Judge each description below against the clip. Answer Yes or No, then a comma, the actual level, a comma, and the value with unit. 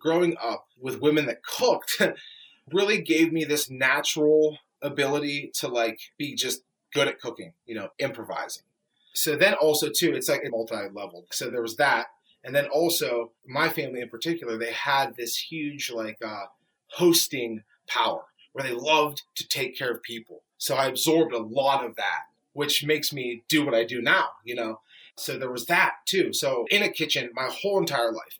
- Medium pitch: Yes, medium, 145 Hz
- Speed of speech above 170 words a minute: Yes, average, 185 wpm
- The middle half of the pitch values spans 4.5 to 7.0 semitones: Yes, average, 5.2 semitones